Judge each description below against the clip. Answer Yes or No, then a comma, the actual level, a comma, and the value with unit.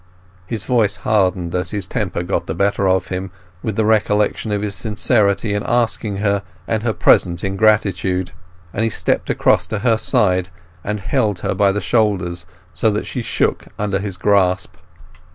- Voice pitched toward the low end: Yes, low, 100 Hz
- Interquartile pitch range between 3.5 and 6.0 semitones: No, narrow, 2.5 semitones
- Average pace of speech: Yes, average, 170 wpm